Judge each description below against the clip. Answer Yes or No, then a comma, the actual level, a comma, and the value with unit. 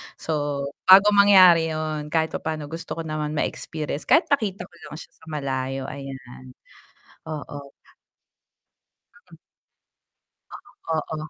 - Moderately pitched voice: Yes, medium, 155 Hz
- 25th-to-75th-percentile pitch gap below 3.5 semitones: Yes, average, 2.7 semitones